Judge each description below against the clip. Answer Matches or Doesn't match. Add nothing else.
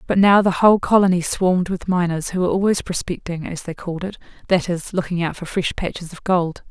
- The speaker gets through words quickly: Matches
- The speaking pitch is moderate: Matches